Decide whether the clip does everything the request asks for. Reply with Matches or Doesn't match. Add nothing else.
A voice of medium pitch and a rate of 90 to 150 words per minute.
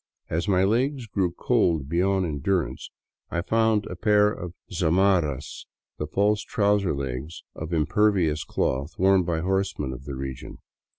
Doesn't match